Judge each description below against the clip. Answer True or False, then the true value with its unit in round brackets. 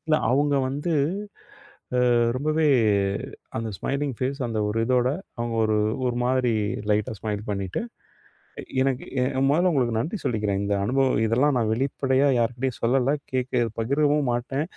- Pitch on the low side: True (125 Hz)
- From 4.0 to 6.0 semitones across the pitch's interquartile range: False (3.4 semitones)